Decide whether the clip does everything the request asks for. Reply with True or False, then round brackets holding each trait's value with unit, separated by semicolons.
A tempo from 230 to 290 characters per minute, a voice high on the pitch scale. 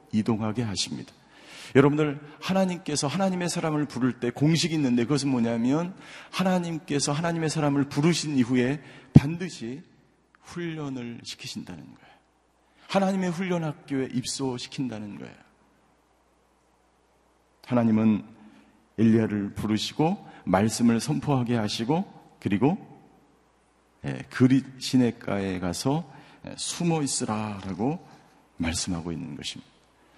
False (275 characters per minute; 135 Hz)